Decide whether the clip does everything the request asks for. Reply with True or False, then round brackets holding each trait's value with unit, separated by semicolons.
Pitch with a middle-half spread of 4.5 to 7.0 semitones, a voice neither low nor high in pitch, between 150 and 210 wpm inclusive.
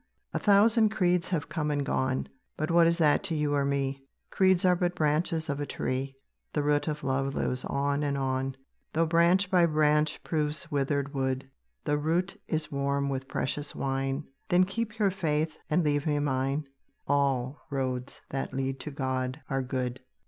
False (3.4 semitones; 145 Hz; 180 wpm)